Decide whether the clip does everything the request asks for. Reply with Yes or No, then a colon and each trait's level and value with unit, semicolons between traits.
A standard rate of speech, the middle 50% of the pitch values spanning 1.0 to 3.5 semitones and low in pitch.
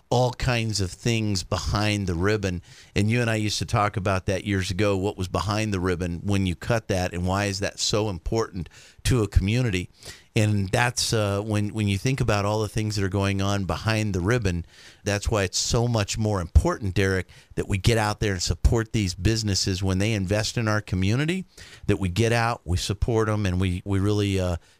No: fast, 215 wpm; narrow, 2.6 semitones; low, 100 Hz